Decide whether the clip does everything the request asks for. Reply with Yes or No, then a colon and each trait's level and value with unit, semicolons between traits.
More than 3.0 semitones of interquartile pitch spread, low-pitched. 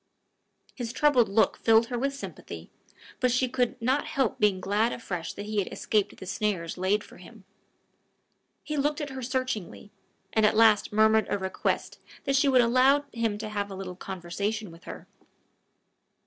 No: average, 4.1 semitones; high, 220 Hz